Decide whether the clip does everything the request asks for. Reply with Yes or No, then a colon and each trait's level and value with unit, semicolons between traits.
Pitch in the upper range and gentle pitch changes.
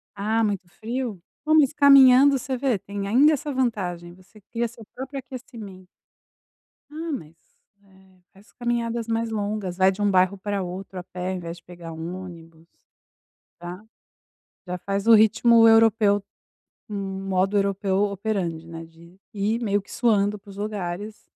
No: high, 200 Hz; average, 3.9 semitones